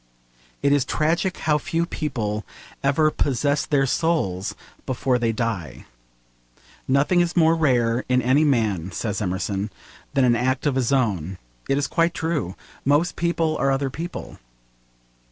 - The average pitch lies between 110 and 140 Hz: Yes, low, 135 Hz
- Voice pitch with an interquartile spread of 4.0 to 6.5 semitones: Yes, average, 5.2 semitones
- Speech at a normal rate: Yes, average, 145 wpm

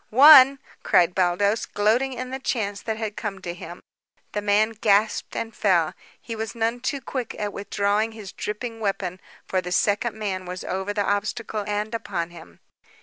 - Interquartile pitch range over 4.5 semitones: No, average, 2.8 semitones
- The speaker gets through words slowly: No, average, 175 wpm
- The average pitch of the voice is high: Yes, high, 210 Hz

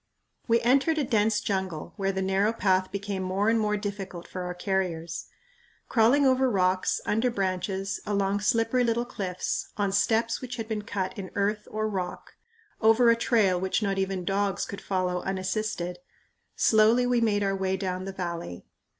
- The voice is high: Yes, high, 200 Hz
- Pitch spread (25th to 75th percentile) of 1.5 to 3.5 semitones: Yes, average, 2.9 semitones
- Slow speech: No, average, 170 wpm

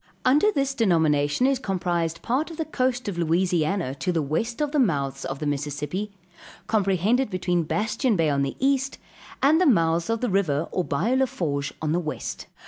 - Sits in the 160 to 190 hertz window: Yes, medium, 185 Hz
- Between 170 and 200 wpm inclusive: Yes, average, 190 wpm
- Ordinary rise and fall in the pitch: No, wide, 8.4 semitones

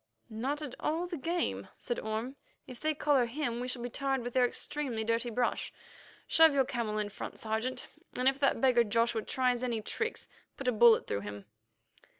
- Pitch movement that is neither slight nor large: Yes, average, 3.1 semitones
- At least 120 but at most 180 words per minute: No, average, 190 wpm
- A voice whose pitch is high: Yes, very high, 250 Hz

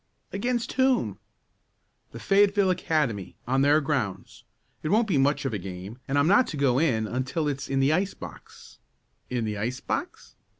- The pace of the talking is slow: No, average, 180 wpm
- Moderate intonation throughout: No, wide, 7.1 semitones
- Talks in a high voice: No, medium, 140 Hz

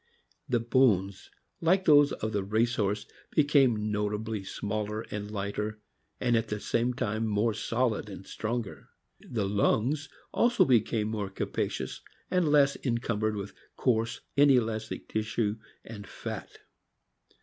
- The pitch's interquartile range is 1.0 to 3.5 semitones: Yes, average, 2.9 semitones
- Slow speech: Yes, slow, 125 wpm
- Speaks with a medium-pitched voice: No, low, 110 Hz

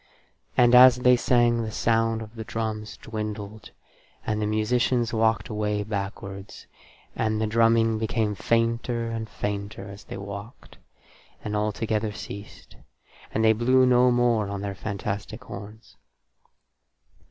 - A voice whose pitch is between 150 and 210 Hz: No, low, 110 Hz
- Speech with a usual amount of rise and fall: No, narrow, 1.8 semitones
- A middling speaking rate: No, slow, 130 wpm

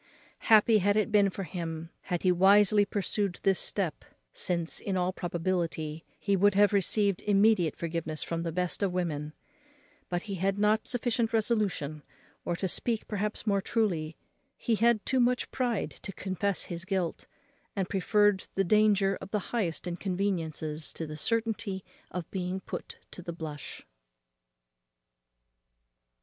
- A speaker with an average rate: Yes, average, 150 wpm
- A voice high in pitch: Yes, high, 195 Hz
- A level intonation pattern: No, average, 3.4 semitones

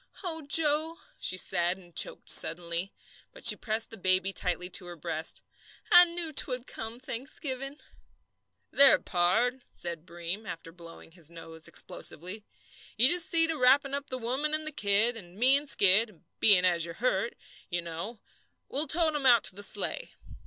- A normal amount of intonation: No, wide, 8.0 semitones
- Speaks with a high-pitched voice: Yes, high, 220 Hz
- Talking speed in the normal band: Yes, average, 170 wpm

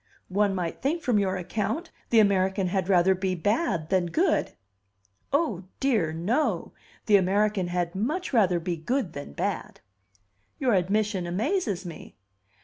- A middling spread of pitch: Yes, average, 4.3 semitones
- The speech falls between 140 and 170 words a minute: Yes, average, 145 wpm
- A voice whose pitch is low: No, high, 195 Hz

